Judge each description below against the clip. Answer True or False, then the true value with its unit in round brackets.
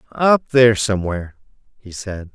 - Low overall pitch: True (110 Hz)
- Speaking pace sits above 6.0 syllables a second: False (5.3 syllables/s)